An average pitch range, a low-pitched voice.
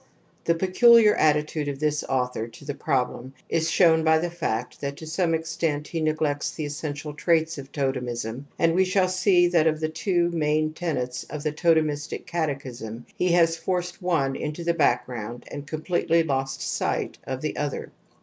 No: average, 3.2 semitones; medium, 155 Hz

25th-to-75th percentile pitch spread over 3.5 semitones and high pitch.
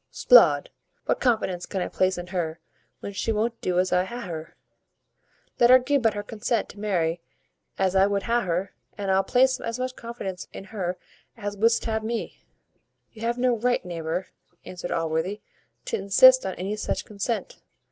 Yes: average, 4.3 semitones; high, 205 Hz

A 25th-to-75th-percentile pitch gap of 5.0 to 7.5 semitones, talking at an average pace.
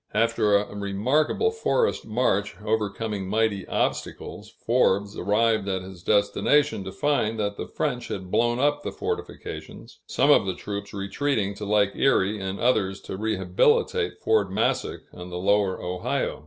No: narrow, 2.6 semitones; average, 150 wpm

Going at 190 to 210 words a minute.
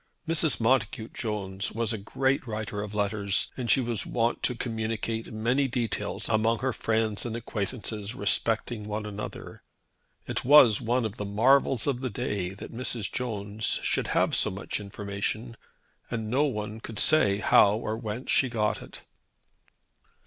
No: average, 155 wpm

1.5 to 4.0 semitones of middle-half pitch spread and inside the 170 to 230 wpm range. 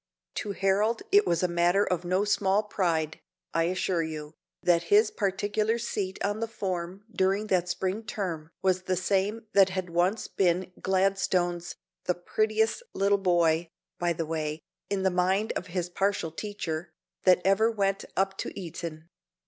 No: average, 2.7 semitones; average, 160 wpm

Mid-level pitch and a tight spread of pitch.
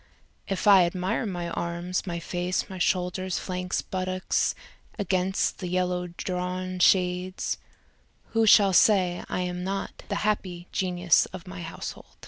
Yes: medium, 180 Hz; narrow, 1.0 semitones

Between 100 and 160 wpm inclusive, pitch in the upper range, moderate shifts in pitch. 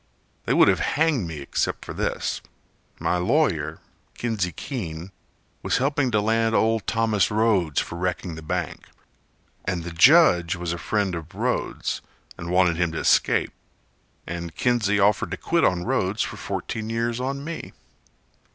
No: average, 155 wpm; low, 100 Hz; average, 5.0 semitones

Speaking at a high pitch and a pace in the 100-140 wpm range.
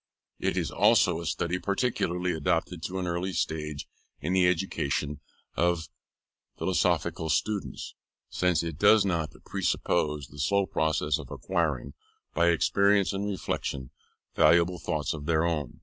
No: very low, 85 Hz; slow, 135 wpm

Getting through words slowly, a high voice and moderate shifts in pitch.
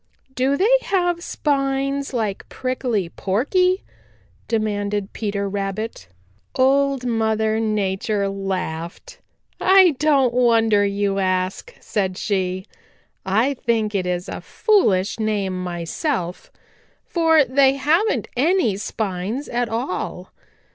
No: slow, 105 wpm; high, 220 Hz; wide, 5.8 semitones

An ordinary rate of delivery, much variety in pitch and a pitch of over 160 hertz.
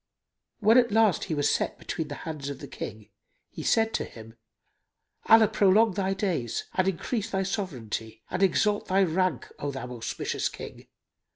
Yes: average, 170 wpm; wide, 6.8 semitones; medium, 185 Hz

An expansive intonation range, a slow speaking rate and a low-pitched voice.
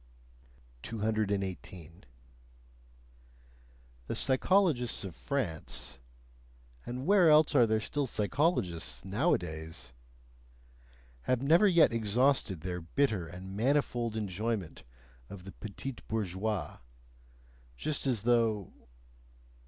Yes: wide, 6.3 semitones; slow, 90 wpm; low, 110 Hz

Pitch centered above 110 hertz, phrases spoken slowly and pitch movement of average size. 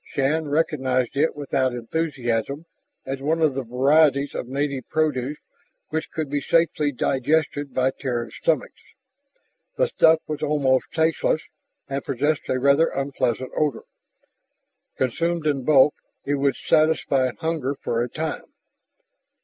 Yes: medium, 140 Hz; slow, 130 wpm; average, 3.0 semitones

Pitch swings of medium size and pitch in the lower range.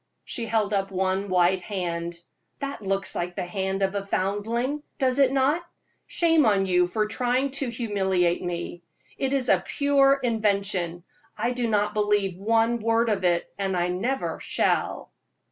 No: average, 4.6 semitones; high, 205 Hz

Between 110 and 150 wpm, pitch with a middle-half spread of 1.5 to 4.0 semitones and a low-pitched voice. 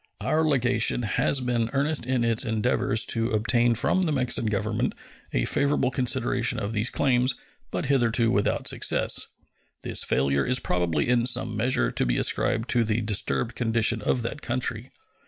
No: average, 160 wpm; narrow, 2.6 semitones; low, 120 Hz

